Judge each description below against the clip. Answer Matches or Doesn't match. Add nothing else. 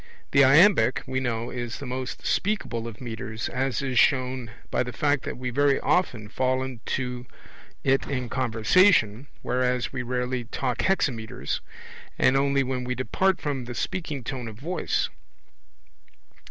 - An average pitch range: Doesn't match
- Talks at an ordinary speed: Matches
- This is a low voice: Matches